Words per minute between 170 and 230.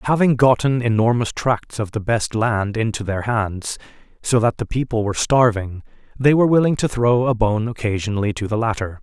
Yes: average, 185 wpm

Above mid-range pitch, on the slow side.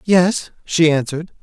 No: medium, 165 Hz; slow, 125 wpm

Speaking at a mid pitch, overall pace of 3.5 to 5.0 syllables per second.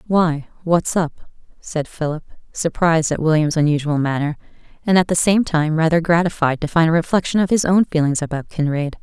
No: medium, 165 Hz; 5.5 syllables/s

